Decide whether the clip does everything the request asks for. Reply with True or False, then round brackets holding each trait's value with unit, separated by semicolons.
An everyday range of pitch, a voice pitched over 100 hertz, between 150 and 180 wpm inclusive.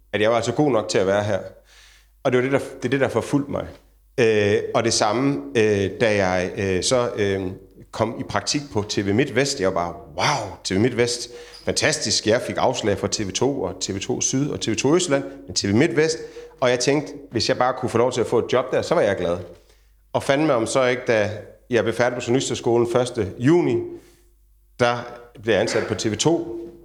False (4.8 semitones; 120 Hz; 215 wpm)